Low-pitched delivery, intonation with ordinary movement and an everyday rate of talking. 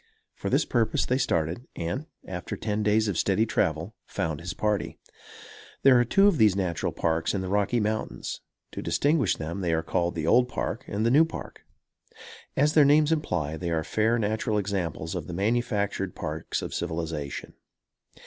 No: low, 100 Hz; wide, 6.0 semitones; average, 175 wpm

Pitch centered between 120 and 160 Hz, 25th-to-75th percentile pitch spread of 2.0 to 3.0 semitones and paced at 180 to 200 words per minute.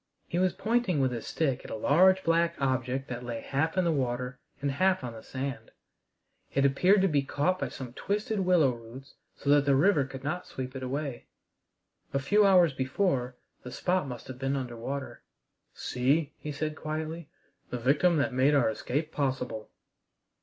No: medium, 140 Hz; average, 4.7 semitones; average, 185 wpm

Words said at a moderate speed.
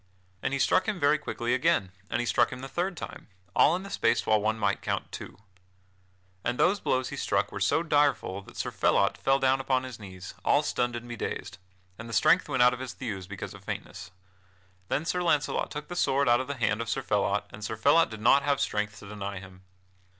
No: fast, 230 wpm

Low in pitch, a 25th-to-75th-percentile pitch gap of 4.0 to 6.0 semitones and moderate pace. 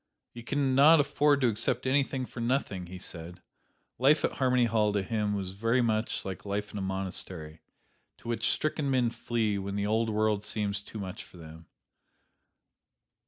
Yes: low, 110 Hz; average, 4.5 semitones; average, 175 wpm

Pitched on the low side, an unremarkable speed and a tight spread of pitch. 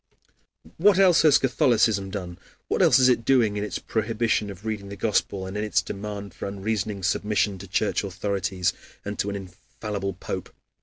Yes: low, 105 Hz; average, 175 wpm; narrow, 2.3 semitones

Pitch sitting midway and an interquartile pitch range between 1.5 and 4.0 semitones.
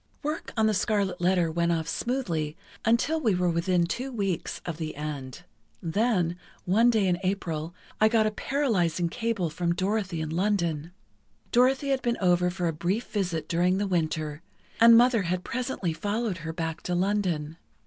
No: medium, 180 Hz; average, 4.7 semitones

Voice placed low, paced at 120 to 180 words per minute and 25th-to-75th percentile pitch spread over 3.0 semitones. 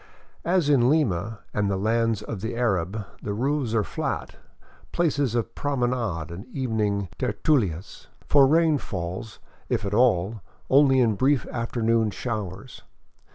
Yes: low, 115 Hz; slow, 135 wpm; average, 4.6 semitones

